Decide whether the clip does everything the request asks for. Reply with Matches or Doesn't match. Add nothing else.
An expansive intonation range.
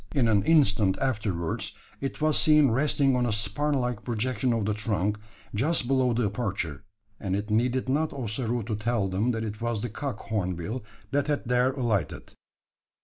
Doesn't match